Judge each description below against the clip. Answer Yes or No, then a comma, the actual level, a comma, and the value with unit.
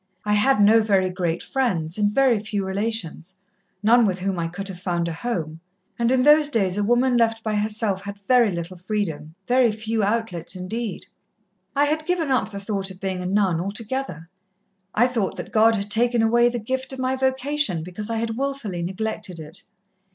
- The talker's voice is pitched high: Yes, high, 210 Hz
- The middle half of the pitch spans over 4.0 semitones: Yes, average, 4.4 semitones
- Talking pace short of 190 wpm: No, average, 195 wpm